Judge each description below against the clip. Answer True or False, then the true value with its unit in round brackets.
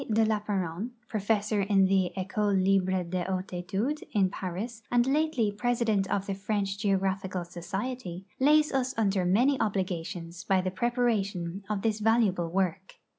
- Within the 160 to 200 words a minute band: False (150 wpm)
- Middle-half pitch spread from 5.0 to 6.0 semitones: False (3.1 semitones)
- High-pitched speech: True (195 Hz)